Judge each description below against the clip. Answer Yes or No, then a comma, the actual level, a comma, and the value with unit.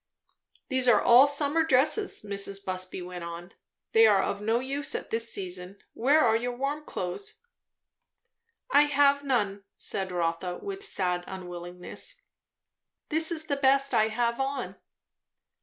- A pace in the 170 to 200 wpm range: No, average, 140 wpm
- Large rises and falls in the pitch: Yes, wide, 7.0 semitones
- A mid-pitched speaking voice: No, high, 230 Hz